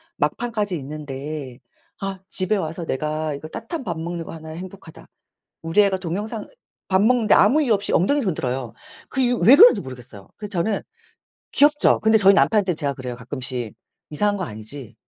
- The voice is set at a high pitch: No, medium, 175 Hz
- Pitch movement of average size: No, wide, 6.5 semitones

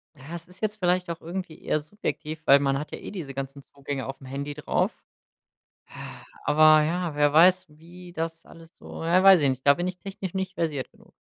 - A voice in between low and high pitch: Yes, medium, 165 Hz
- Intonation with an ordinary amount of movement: Yes, average, 4.0 semitones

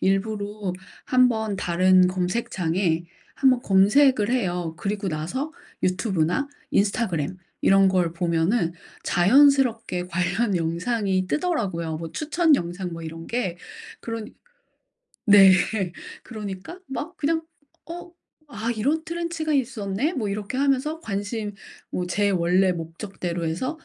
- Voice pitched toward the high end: Yes, high, 200 Hz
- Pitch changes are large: Yes, wide, 6.0 semitones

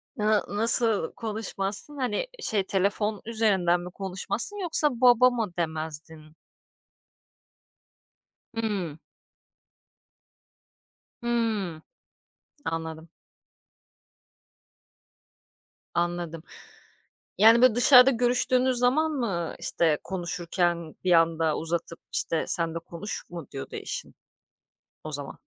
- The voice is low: No, high, 195 Hz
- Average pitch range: No, wide, 5.7 semitones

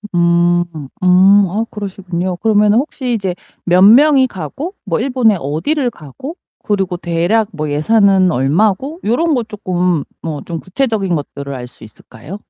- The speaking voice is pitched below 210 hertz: Yes, high, 190 Hz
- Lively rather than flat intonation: No, average, 4.7 semitones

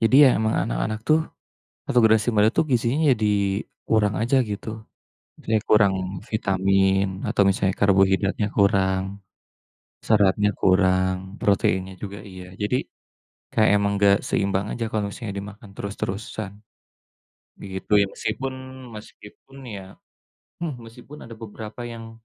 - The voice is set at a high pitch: No, low, 105 Hz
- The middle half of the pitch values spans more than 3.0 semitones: No, narrow, 2.5 semitones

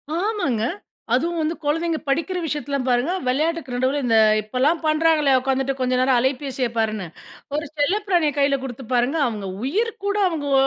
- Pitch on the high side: Yes, very high, 285 Hz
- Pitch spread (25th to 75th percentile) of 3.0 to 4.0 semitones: No, average, 4.5 semitones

